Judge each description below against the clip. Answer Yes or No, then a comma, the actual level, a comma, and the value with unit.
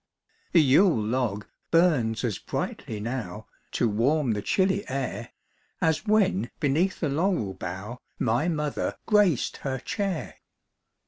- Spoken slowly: Yes, slow, 125 wpm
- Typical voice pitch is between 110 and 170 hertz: Yes, low, 135 Hz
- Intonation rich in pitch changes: Yes, wide, 7.3 semitones